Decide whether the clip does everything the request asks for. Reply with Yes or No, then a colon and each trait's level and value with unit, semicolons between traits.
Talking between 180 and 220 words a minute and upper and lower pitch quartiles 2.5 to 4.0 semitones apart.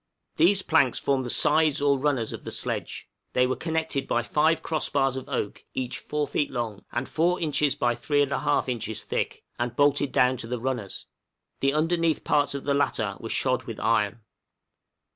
Yes: average, 185 wpm; average, 3.6 semitones